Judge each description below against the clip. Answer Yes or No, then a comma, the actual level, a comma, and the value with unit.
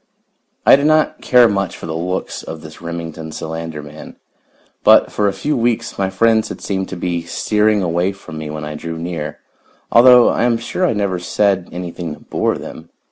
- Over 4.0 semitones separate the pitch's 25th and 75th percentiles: Yes, average, 4.6 semitones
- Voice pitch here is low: Yes, very low, 90 Hz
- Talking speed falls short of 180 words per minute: No, average, 195 wpm